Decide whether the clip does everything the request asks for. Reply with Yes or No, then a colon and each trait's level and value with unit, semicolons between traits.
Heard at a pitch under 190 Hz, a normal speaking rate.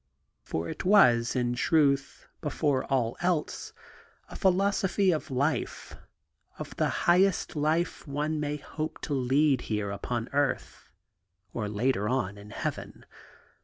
No: medium, 140 Hz; slow, 130 wpm